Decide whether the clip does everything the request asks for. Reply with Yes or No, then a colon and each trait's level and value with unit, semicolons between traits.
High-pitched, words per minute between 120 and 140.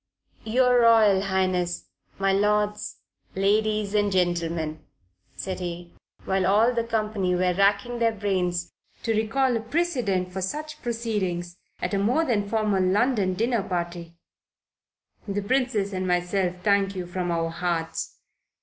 Yes: high, 200 Hz; slow, 135 wpm